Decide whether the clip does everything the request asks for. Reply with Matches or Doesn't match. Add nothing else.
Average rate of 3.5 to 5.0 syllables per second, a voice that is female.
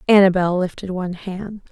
Doesn't match